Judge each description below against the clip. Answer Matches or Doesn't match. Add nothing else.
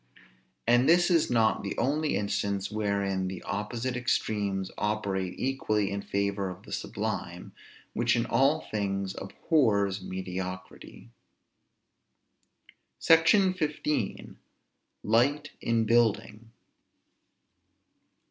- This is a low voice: Matches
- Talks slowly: Matches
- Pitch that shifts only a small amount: Doesn't match